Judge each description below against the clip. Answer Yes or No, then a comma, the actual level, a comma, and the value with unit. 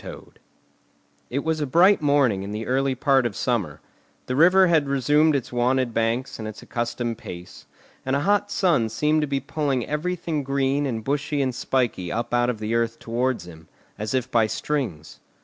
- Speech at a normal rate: Yes, average, 185 wpm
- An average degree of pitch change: Yes, average, 4.2 semitones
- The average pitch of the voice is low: Yes, low, 130 Hz